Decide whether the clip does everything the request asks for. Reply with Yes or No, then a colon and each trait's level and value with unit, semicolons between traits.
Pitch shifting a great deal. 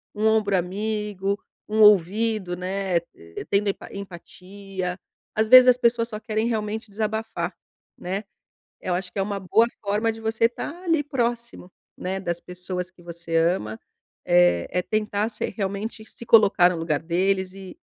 No: average, 3.3 semitones